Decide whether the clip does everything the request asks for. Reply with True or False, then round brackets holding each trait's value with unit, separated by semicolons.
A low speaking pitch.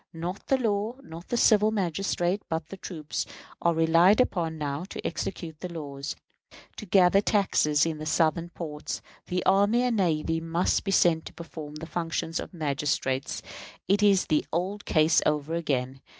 False (170 Hz)